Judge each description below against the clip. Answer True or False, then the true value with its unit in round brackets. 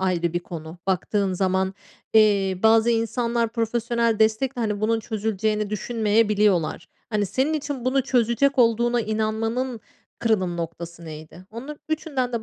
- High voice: True (220 Hz)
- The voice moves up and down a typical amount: True (3.7 semitones)